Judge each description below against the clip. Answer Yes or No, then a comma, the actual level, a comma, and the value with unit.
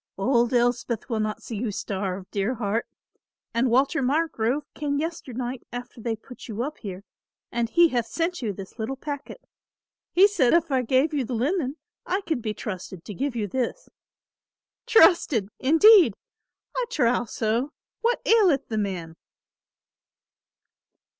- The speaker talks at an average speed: Yes, average, 150 wpm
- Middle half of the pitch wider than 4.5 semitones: Yes, average, 5.3 semitones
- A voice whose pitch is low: No, high, 245 Hz